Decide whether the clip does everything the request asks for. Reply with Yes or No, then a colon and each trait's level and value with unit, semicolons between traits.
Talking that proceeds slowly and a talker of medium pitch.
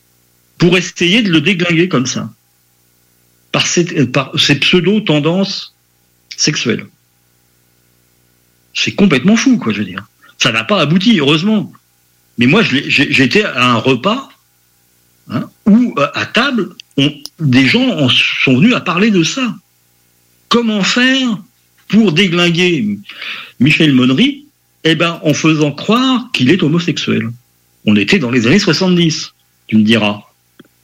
Yes: slow, 130 wpm; medium, 145 Hz